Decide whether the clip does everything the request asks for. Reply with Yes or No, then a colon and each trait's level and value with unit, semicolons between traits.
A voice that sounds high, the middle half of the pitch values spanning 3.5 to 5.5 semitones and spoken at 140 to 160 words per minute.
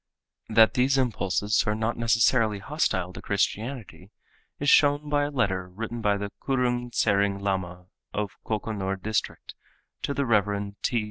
No: low, 110 Hz; average, 3.8 semitones; average, 145 wpm